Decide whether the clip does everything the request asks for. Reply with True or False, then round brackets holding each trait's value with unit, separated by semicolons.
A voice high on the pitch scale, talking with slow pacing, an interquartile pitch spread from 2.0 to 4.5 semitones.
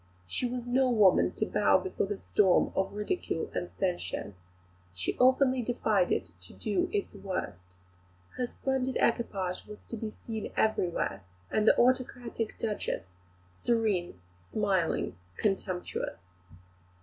False (210 Hz; 125 wpm; 5.2 semitones)